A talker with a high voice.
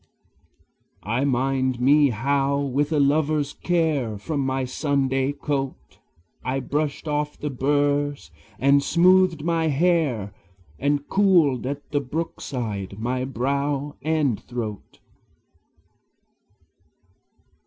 No: medium, 140 Hz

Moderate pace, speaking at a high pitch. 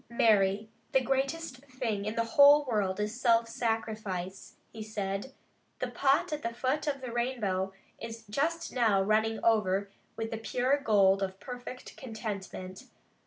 Yes: average, 150 wpm; high, 225 Hz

